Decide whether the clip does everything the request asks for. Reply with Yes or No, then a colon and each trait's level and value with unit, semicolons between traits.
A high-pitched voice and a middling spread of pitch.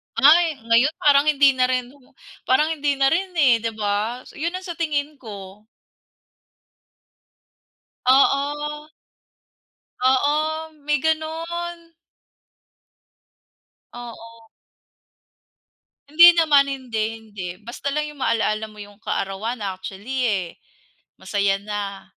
No: very high, 270 Hz; wide, 5.7 semitones